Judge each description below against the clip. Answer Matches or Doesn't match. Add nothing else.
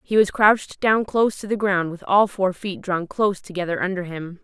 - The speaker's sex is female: Matches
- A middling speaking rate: Doesn't match